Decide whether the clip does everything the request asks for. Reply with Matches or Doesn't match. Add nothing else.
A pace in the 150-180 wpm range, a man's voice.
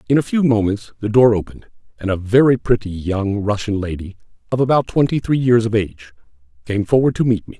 Doesn't match